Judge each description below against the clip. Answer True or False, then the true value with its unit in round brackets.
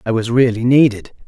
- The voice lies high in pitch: False (120 Hz)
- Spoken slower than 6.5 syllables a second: True (5.7 syllables/s)